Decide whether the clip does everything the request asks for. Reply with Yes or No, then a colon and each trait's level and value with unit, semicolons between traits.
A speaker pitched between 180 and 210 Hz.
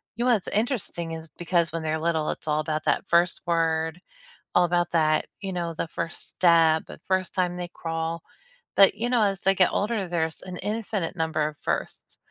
No: medium, 170 Hz